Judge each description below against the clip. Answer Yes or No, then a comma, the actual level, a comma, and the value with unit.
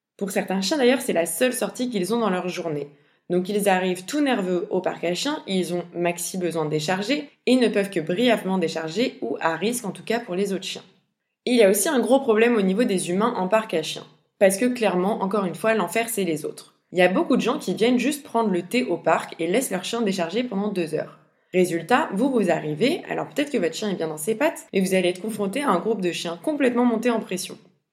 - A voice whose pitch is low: No, high, 195 Hz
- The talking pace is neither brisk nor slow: No, fast, 260 wpm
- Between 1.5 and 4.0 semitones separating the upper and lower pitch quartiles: No, average, 4.9 semitones